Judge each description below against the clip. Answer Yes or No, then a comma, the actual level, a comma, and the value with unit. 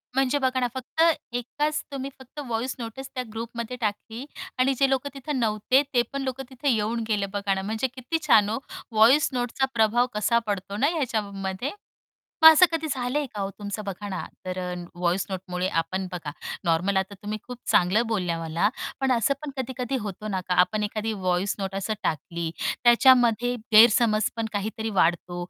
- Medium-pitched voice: No, high, 220 Hz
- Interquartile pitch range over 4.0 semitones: Yes, average, 4.6 semitones